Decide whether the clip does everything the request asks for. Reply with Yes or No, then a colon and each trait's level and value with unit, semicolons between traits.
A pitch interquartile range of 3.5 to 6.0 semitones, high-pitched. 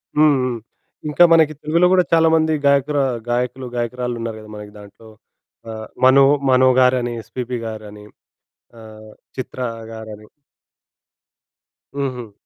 No: average, 4.1 semitones; low, 125 Hz